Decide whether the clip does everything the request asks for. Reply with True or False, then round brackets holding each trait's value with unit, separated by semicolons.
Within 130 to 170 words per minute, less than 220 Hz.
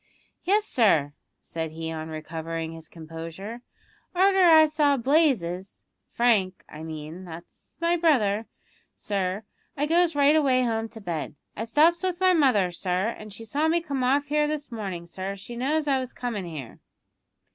False (165 wpm; 225 Hz)